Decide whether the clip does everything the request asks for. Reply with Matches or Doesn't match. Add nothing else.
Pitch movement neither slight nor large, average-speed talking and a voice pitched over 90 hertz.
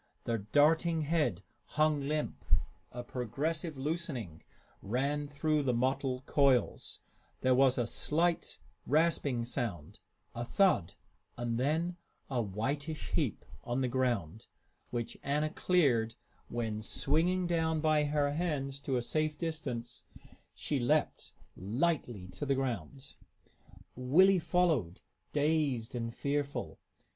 Doesn't match